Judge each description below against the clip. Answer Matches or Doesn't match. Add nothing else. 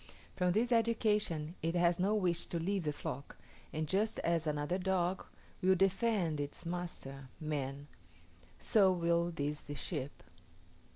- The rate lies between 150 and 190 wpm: Doesn't match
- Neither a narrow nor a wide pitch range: Matches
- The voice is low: Doesn't match